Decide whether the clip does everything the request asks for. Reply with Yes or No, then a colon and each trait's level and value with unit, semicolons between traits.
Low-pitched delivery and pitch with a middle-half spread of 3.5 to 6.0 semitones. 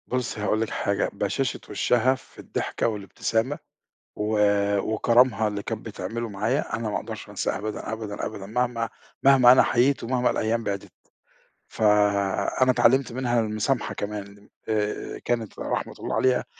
No: low, 110 Hz; average, 2.8 semitones